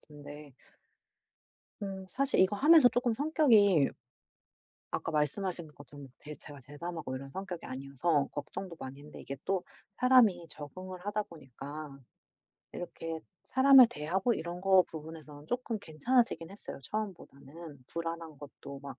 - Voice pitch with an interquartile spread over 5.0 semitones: Yes, wide, 5.6 semitones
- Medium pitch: Yes, medium, 165 Hz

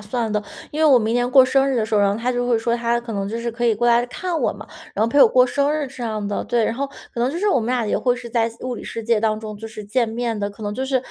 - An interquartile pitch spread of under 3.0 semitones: Yes, narrow, 2.4 semitones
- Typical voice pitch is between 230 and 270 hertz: Yes, high, 235 Hz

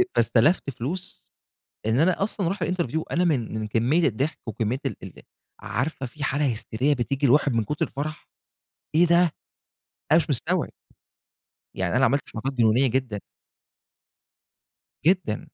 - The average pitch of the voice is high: No, low, 135 Hz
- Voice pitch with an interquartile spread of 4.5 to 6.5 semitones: Yes, wide, 5.4 semitones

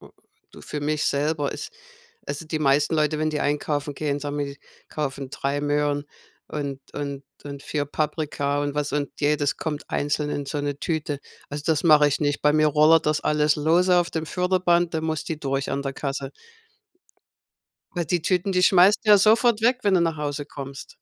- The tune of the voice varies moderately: No, narrow, 2.0 semitones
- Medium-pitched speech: Yes, medium, 150 Hz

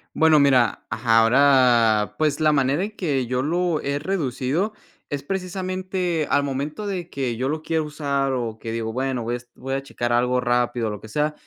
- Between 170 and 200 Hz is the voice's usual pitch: No, medium, 140 Hz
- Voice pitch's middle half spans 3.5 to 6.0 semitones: Yes, average, 4.3 semitones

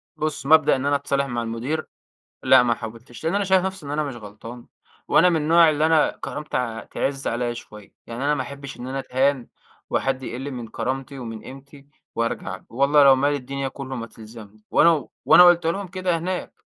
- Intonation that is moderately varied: Yes, average, 4.1 semitones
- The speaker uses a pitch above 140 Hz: No, low, 135 Hz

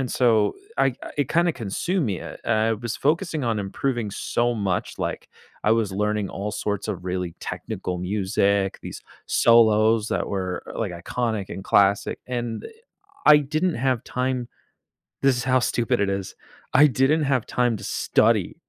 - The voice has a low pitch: Yes, low, 115 Hz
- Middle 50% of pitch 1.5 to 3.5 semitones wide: No, average, 4.3 semitones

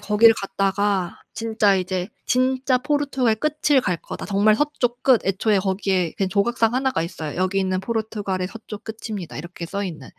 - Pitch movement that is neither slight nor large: Yes, average, 4.2 semitones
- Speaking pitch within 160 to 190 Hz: No, high, 205 Hz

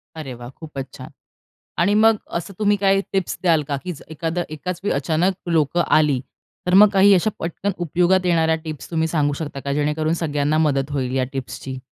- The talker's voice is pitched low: No, medium, 160 Hz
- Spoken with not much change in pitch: No, average, 3.9 semitones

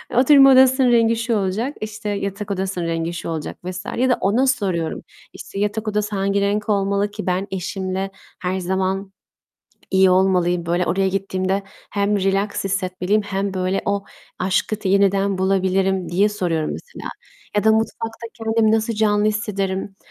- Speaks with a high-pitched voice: Yes, high, 195 Hz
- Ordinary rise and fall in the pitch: No, narrow, 2.1 semitones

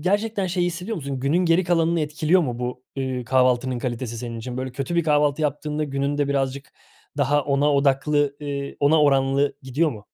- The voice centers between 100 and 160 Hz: Yes, medium, 140 Hz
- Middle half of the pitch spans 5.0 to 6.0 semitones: No, average, 3.2 semitones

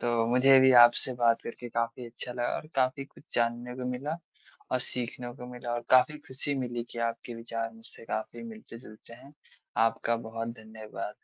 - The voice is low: Yes, low, 120 Hz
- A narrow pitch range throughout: Yes, narrow, 1.7 semitones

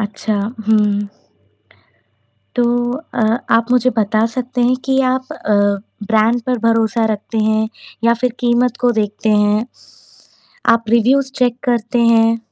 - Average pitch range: No, narrow, 2.3 semitones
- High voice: Yes, high, 230 Hz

